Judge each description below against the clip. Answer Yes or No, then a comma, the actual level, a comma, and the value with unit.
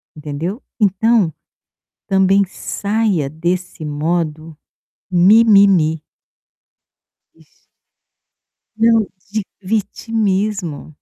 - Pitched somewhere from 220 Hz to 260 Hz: No, high, 190 Hz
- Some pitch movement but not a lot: Yes, average, 4.9 semitones